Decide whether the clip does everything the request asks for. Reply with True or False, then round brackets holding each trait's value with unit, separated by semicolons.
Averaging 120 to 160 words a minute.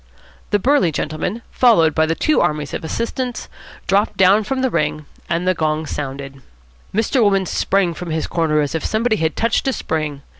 False (185 wpm)